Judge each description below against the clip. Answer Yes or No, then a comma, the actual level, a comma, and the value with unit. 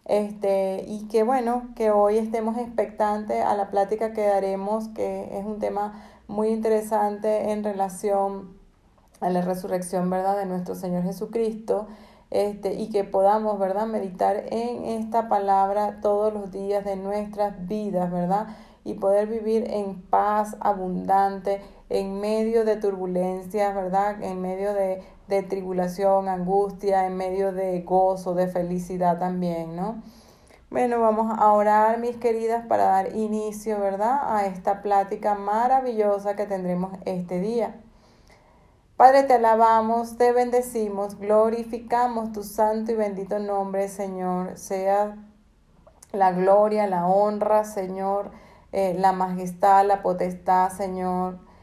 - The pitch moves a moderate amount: No, narrow, 1.9 semitones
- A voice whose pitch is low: No, high, 200 Hz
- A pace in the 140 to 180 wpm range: No, average, 130 wpm